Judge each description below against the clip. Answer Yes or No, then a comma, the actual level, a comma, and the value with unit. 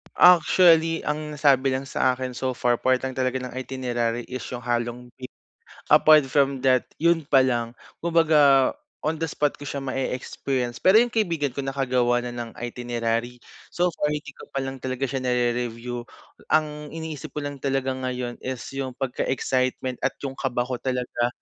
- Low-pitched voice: Yes, low, 130 Hz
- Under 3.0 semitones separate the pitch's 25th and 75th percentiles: Yes, narrow, 2.6 semitones